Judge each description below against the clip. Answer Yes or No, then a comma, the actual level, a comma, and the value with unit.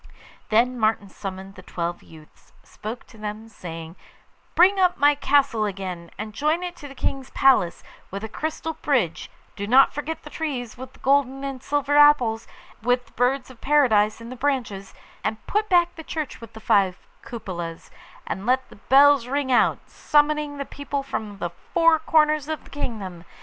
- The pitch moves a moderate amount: No, wide, 5.7 semitones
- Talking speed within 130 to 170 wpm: No, average, 180 wpm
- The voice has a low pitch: No, very high, 255 Hz